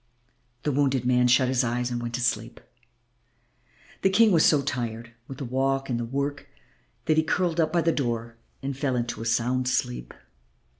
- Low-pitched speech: Yes, low, 130 Hz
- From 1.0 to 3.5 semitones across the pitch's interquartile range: Yes, average, 3.1 semitones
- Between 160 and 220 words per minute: Yes, average, 190 wpm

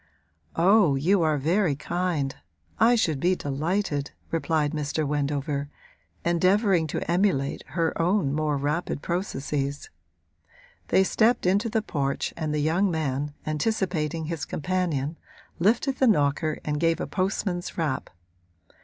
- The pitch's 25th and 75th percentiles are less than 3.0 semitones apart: No, average, 4.2 semitones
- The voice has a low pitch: No, medium, 160 Hz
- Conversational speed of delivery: No, slow, 125 wpm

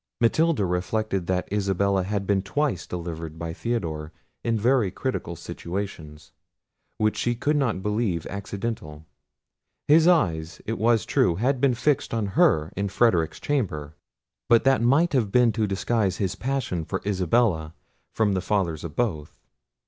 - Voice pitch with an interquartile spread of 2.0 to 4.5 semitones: No, wide, 5.6 semitones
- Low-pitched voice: Yes, low, 100 Hz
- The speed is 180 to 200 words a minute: No, average, 150 wpm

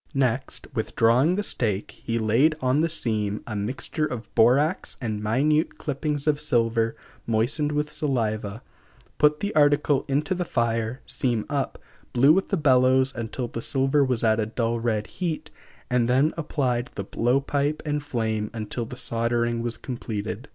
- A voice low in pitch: Yes, low, 125 Hz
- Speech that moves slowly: No, average, 160 wpm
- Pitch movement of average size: Yes, average, 4.3 semitones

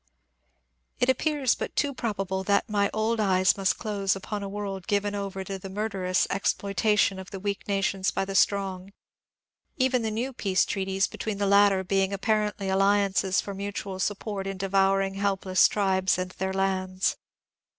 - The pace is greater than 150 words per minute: Yes, average, 170 wpm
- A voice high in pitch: Yes, high, 195 Hz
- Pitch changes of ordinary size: No, narrow, 1.4 semitones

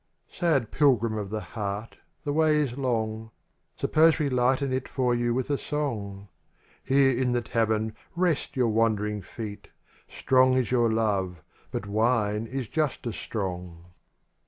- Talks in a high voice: No, low, 115 Hz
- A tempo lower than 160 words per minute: Yes, average, 150 wpm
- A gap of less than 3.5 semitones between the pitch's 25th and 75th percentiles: No, average, 3.9 semitones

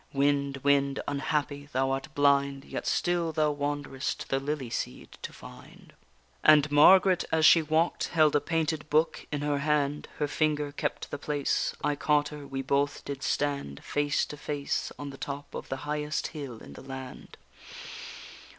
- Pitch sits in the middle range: Yes, medium, 145 Hz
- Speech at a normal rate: Yes, average, 170 wpm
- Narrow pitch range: Yes, narrow, 1.3 semitones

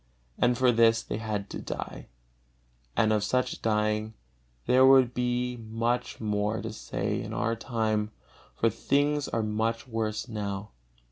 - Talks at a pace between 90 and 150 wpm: Yes, average, 145 wpm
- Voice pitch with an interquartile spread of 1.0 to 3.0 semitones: Yes, narrow, 2.4 semitones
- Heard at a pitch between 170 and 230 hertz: No, low, 115 Hz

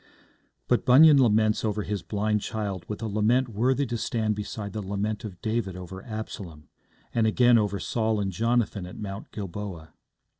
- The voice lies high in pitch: No, low, 105 Hz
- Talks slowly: No, average, 165 wpm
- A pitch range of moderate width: No, narrow, 2.3 semitones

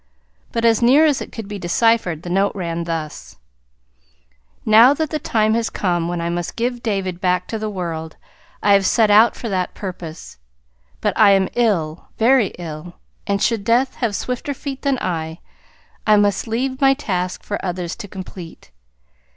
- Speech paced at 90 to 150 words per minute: No, average, 175 wpm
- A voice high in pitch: Yes, high, 200 Hz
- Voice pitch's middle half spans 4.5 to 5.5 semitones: Yes, average, 4.8 semitones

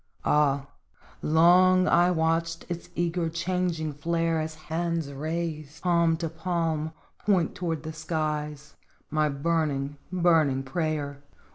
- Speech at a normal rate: No, slow, 115 wpm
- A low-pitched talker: No, medium, 160 Hz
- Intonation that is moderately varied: No, narrow, 2.0 semitones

